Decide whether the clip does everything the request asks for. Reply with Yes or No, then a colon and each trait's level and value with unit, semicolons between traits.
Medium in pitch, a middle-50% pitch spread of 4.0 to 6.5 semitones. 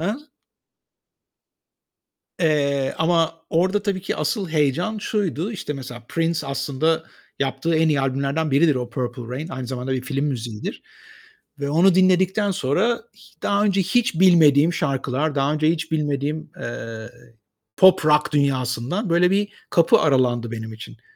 Yes: medium, 150 Hz; average, 4.6 semitones